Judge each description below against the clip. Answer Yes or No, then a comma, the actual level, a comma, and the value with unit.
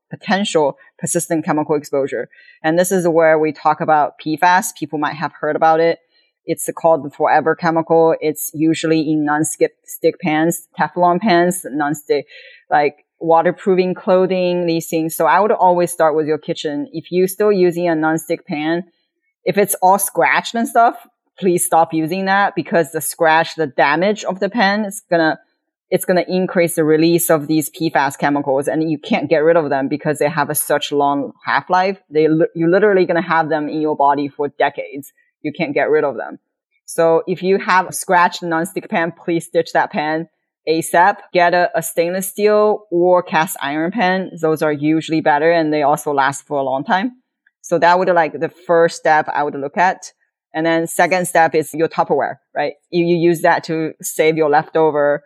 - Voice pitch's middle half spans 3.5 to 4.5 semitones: No, average, 2.7 semitones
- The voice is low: No, medium, 165 Hz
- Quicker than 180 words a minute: Yes, average, 190 wpm